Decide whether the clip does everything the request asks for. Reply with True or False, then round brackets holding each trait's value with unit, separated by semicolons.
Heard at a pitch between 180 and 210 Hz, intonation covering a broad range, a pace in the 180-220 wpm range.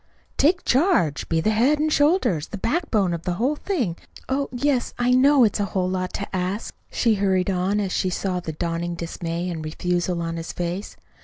True (190 Hz; 6.3 semitones; 200 wpm)